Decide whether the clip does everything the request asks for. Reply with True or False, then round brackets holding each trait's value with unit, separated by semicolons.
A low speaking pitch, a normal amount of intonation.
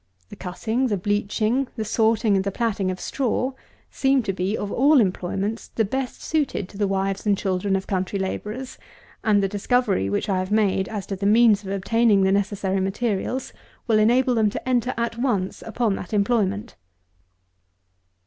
False (210 Hz; 3.3 semitones)